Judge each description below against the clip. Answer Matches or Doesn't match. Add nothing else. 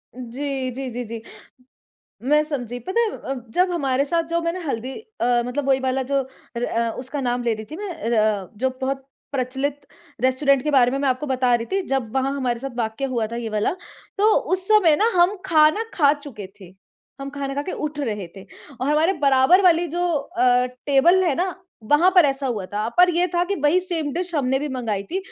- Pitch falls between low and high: Doesn't match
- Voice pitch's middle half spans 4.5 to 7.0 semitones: Matches